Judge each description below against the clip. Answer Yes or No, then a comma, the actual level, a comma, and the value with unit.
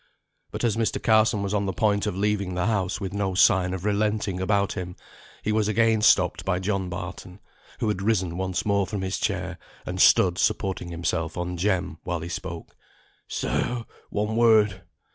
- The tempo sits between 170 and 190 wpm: Yes, average, 180 wpm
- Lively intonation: No, average, 2.7 semitones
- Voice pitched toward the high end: No, very low, 95 Hz